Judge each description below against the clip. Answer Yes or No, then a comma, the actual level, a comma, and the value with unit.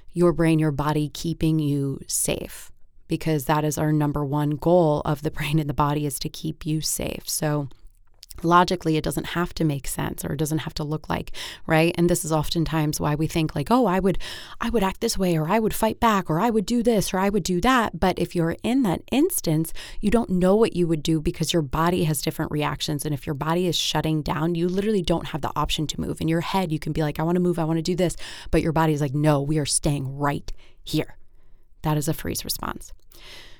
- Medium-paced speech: No, fast, 245 wpm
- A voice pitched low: No, medium, 160 Hz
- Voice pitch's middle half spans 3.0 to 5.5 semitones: No, narrow, 2.6 semitones